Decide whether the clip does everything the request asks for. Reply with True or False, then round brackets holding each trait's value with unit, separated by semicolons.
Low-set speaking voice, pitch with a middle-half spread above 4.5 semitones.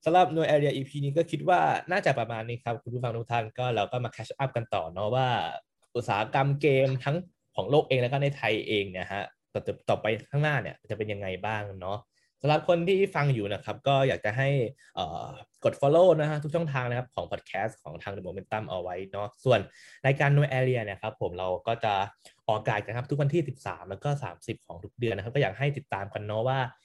True (125 Hz; 4.9 semitones)